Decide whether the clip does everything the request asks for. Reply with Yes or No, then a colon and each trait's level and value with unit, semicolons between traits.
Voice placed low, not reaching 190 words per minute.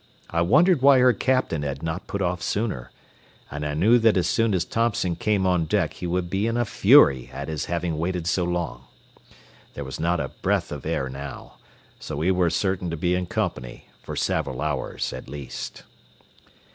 No: very low, 90 Hz; average, 195 wpm